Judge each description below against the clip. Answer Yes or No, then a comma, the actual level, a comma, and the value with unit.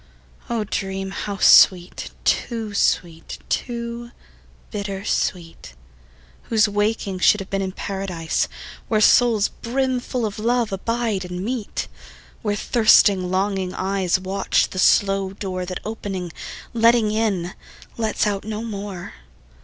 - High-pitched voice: Yes, high, 200 Hz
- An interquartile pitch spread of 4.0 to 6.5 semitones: No, average, 3.0 semitones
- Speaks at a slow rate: Yes, slow, 120 wpm